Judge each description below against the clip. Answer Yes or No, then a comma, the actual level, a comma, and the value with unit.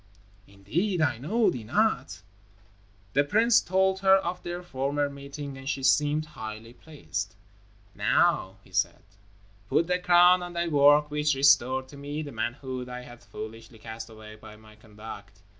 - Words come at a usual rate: Yes, average, 160 wpm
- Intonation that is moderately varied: No, wide, 6.9 semitones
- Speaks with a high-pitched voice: No, medium, 140 Hz